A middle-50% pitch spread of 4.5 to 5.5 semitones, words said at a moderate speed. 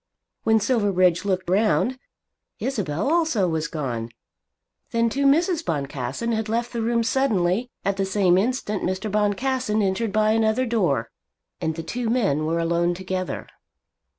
Yes: average, 4.9 semitones; average, 145 wpm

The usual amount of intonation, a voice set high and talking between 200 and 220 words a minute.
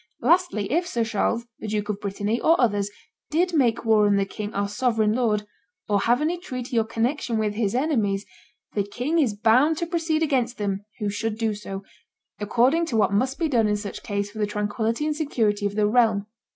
Yes: average, 4.1 semitones; high, 225 Hz; fast, 205 wpm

